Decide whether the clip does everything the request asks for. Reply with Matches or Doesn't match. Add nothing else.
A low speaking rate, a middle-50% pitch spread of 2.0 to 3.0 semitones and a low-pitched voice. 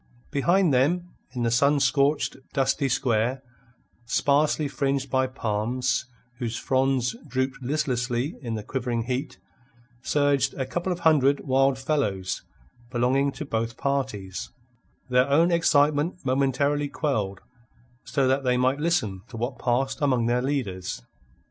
Matches